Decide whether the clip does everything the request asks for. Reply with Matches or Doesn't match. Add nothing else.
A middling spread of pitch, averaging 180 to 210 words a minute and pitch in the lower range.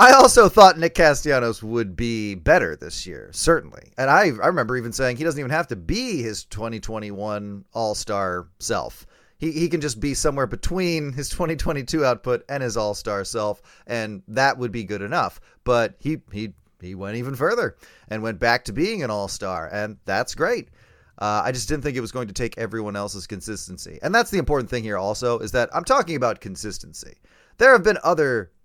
Doesn't match